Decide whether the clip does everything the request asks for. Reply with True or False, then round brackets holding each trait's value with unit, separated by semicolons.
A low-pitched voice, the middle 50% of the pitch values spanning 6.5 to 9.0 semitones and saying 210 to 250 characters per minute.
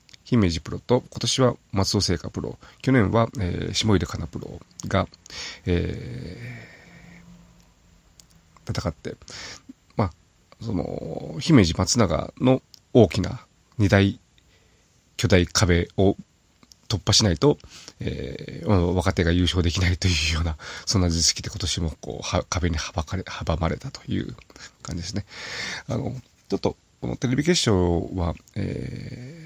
False (100 Hz; 5.8 semitones; 240 characters per minute)